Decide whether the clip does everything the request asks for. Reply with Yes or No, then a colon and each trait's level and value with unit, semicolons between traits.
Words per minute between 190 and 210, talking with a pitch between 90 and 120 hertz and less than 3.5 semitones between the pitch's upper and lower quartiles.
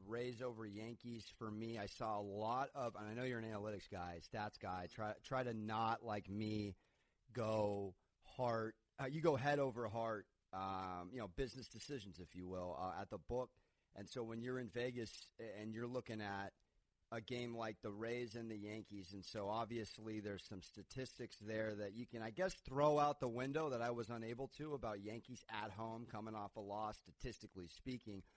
Yes: average, 200 wpm; low, 110 Hz; average, 2.9 semitones